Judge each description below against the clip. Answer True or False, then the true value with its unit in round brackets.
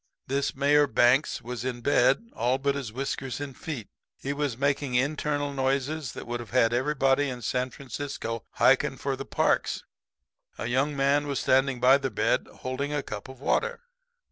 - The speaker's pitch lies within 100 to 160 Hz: True (135 Hz)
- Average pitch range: False (2.3 semitones)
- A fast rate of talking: False (175 wpm)